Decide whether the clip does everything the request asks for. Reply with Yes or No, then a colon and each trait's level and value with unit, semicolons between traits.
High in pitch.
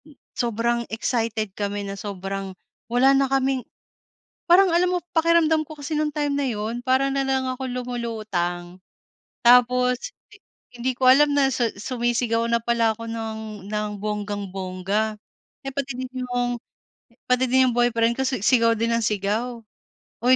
Yes: high, 240 Hz